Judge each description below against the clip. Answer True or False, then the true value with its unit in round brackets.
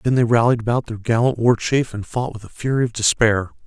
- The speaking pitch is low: True (115 Hz)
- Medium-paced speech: False (245 wpm)